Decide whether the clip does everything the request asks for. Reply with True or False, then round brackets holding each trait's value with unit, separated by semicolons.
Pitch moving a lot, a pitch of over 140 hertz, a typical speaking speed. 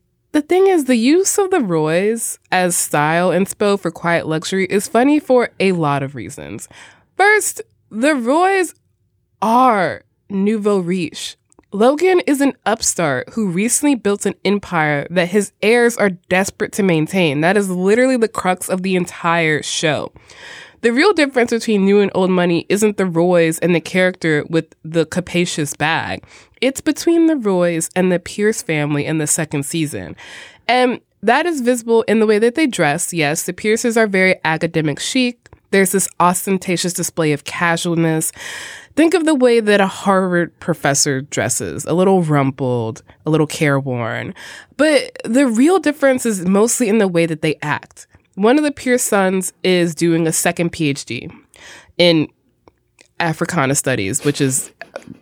True (6.2 semitones; 185 Hz; 160 wpm)